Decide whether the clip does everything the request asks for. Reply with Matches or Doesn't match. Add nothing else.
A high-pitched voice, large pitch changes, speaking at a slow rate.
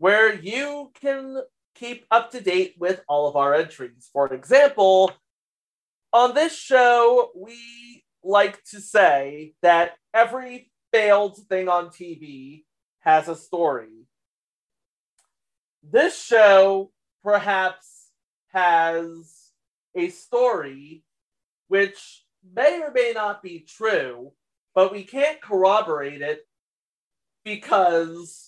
Matches